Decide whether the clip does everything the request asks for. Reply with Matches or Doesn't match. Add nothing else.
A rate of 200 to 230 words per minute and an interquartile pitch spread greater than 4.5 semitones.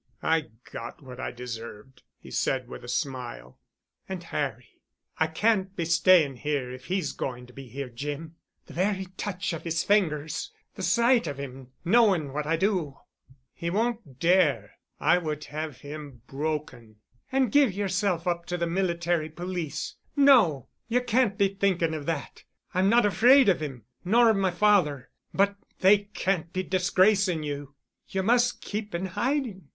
Doesn't match